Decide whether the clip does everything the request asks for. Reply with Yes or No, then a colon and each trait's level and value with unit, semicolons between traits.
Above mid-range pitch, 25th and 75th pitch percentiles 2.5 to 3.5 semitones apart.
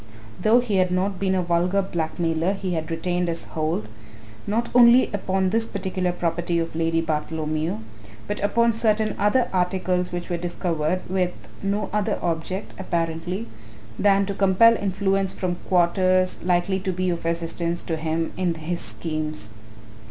No: medium, 180 Hz; average, 2.8 semitones